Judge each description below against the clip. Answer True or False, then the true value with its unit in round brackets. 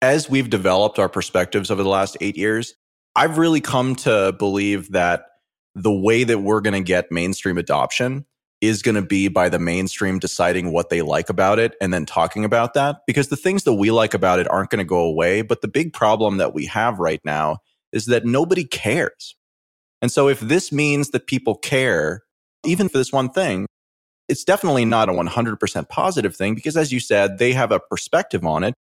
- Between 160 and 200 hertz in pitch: False (110 Hz)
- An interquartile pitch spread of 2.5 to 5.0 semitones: False (5.5 semitones)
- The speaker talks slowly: False (205 wpm)